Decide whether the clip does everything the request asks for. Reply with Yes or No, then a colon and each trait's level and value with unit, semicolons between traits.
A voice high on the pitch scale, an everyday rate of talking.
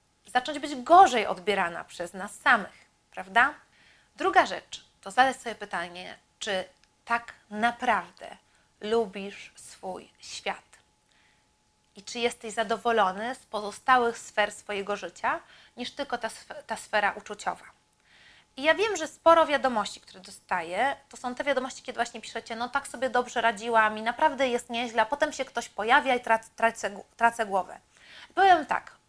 Yes: high, 235 Hz; average, 145 wpm